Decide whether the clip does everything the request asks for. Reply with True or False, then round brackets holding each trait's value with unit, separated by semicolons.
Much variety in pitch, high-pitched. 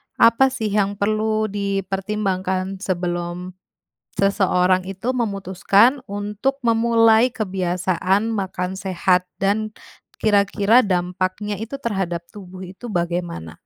False (2.8 semitones; 195 Hz)